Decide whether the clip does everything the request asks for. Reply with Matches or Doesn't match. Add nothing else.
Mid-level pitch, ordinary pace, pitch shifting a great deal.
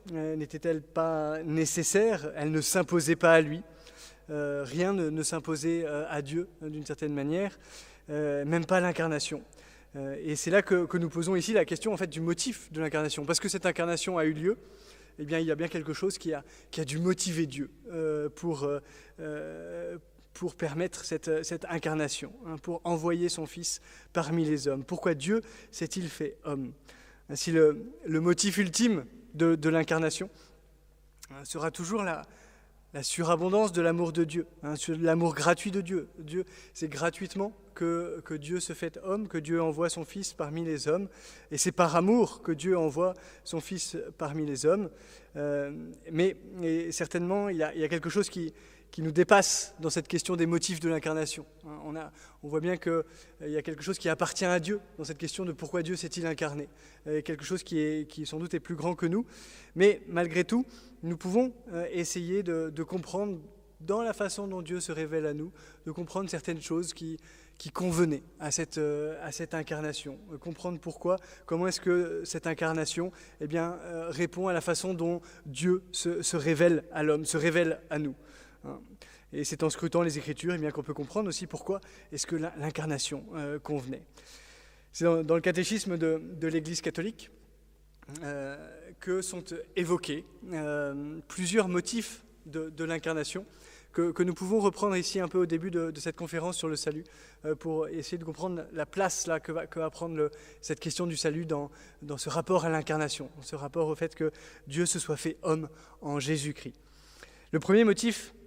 Doesn't match